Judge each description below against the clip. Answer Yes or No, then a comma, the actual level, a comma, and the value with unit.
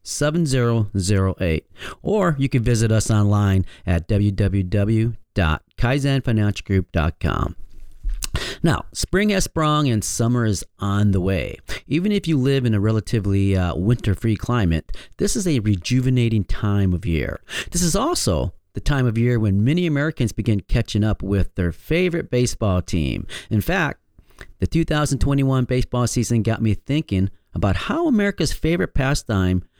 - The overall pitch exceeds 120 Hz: No, low, 110 Hz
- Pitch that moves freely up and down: Yes, wide, 6.1 semitones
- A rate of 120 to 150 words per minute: Yes, average, 140 wpm